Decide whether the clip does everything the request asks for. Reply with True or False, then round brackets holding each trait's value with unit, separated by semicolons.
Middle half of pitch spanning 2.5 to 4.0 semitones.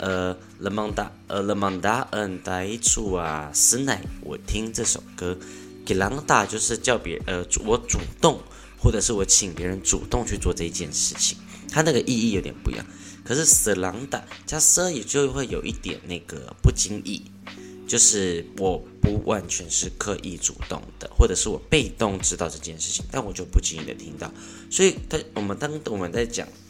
True (3.6 semitones)